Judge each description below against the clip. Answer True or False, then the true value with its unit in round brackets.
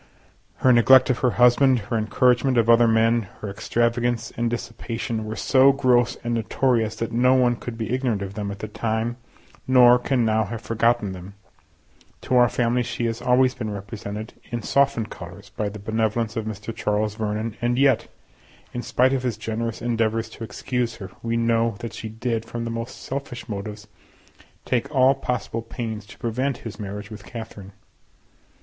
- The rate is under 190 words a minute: True (180 wpm)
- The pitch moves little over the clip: True (2.1 semitones)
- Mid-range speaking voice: False (115 Hz)